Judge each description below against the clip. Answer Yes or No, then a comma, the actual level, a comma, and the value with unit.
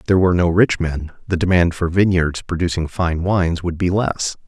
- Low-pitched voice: Yes, very low, 85 Hz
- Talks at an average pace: No, fast, 215 wpm